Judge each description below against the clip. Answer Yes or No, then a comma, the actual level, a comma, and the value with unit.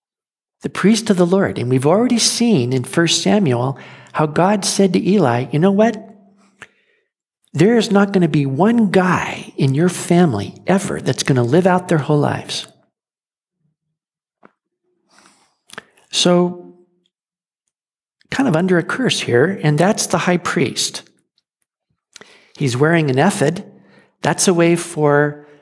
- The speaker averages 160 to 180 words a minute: No, average, 140 wpm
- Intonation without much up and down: No, average, 5.0 semitones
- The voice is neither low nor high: Yes, medium, 180 Hz